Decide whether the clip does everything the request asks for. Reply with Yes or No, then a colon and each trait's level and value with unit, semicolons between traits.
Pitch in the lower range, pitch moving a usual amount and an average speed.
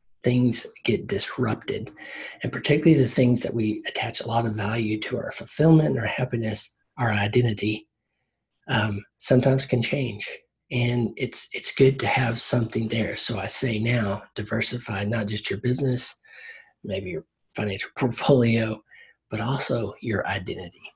Yes: low, 120 Hz; average, 3.2 semitones; average, 145 wpm